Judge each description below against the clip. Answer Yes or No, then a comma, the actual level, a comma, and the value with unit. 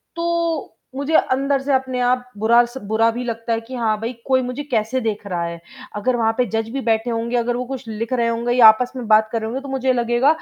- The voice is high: Yes, high, 240 Hz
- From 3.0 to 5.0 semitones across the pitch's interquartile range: No, narrow, 2.5 semitones